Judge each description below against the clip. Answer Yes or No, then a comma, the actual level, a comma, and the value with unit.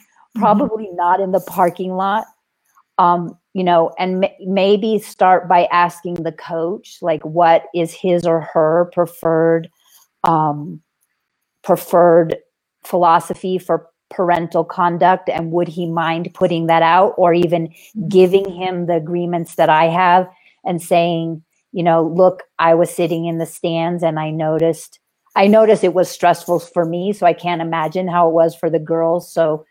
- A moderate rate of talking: Yes, average, 160 wpm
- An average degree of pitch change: No, narrow, 1.9 semitones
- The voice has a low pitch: No, medium, 175 Hz